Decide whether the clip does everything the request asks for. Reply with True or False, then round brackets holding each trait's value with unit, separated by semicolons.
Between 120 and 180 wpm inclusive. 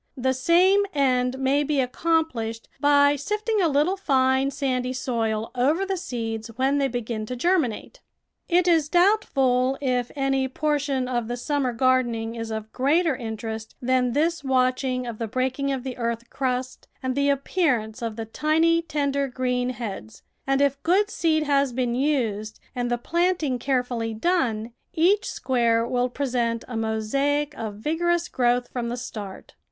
True (165 wpm)